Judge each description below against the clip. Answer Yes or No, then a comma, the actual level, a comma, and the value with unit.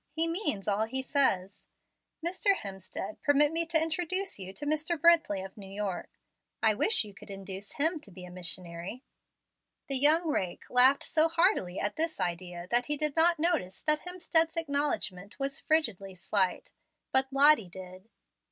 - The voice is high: Yes, very high, 265 Hz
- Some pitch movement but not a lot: No, wide, 8.8 semitones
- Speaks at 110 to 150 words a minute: No, average, 165 wpm